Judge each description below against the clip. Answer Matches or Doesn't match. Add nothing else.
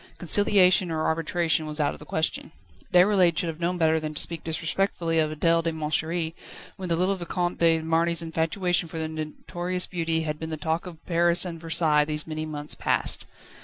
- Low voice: Doesn't match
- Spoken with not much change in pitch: Matches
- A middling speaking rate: Matches